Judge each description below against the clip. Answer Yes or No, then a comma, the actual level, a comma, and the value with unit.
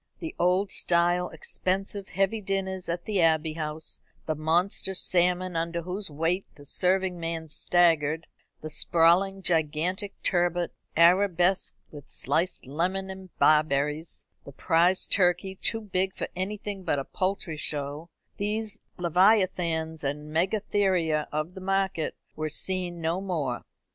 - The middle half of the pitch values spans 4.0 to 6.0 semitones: No, average, 3.0 semitones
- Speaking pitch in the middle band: Yes, medium, 175 Hz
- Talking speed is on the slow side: Yes, slow, 130 wpm